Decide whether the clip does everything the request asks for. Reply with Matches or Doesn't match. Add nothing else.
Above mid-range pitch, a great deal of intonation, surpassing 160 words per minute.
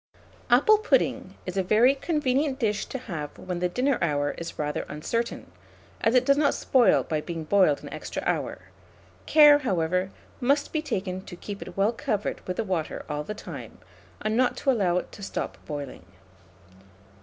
Matches